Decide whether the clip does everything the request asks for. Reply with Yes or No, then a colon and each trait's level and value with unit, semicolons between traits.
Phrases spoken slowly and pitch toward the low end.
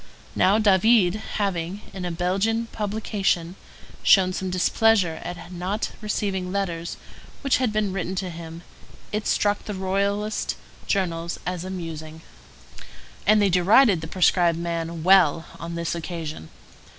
No: slow, 130 wpm; medium, 185 Hz